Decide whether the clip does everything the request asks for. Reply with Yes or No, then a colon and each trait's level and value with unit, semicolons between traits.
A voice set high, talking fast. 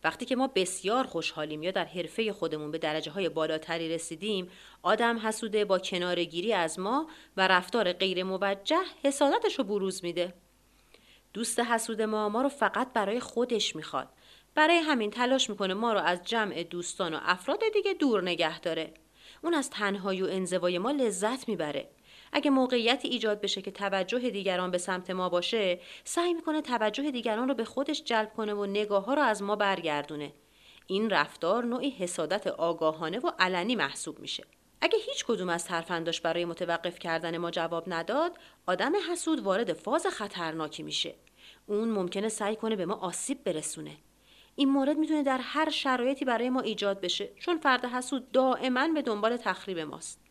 Yes: high, 210 Hz; fast, 165 wpm